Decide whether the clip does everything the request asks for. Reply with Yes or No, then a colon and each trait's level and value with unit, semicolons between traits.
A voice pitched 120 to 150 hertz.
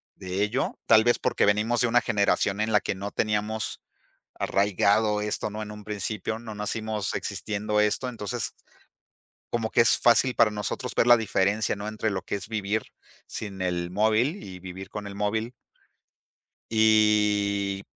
No: low, 105 Hz